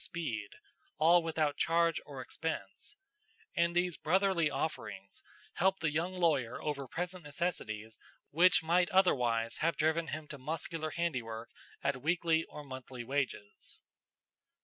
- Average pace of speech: No, slow, 125 wpm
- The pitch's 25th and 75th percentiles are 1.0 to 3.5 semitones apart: No, average, 4.5 semitones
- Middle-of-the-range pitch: Yes, medium, 155 Hz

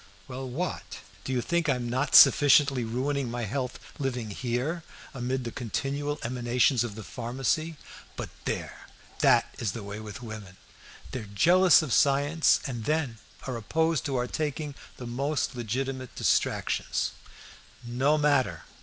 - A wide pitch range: No, average, 3.5 semitones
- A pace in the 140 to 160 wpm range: Yes, average, 145 wpm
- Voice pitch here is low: Yes, low, 130 Hz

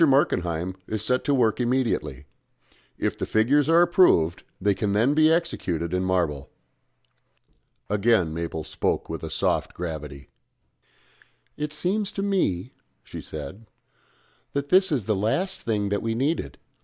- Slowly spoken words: No, average, 145 wpm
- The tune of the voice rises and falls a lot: Yes, wide, 8.5 semitones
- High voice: No, low, 110 Hz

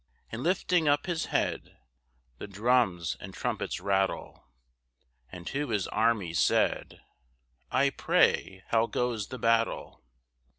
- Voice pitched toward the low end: Yes, low, 115 Hz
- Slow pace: Yes, slow, 120 wpm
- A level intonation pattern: No, wide, 5.6 semitones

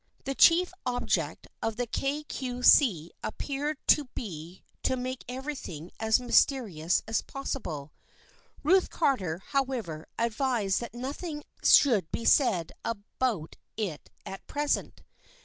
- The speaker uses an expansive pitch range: Yes, wide, 6.4 semitones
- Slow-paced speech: Yes, slow, 125 wpm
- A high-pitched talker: Yes, high, 245 Hz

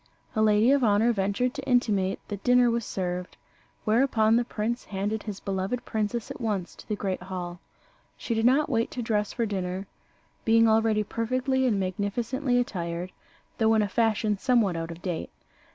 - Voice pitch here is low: No, high, 220 Hz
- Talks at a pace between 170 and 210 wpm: Yes, average, 175 wpm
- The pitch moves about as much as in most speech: Yes, average, 3.6 semitones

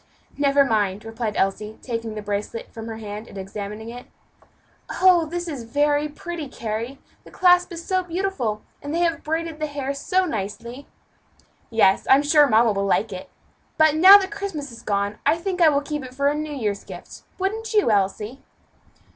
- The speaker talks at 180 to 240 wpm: Yes, average, 185 wpm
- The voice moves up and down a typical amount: No, wide, 7.2 semitones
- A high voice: Yes, very high, 275 Hz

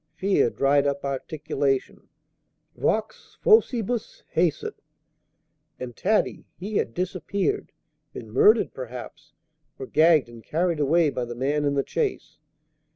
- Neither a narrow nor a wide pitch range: No, wide, 6.4 semitones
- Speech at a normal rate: No, slow, 120 wpm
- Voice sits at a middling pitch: Yes, medium, 155 Hz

